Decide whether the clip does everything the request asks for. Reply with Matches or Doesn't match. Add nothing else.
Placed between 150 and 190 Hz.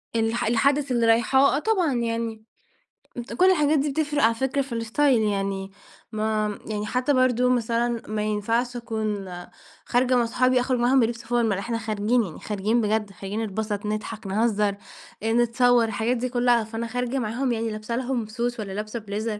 Doesn't match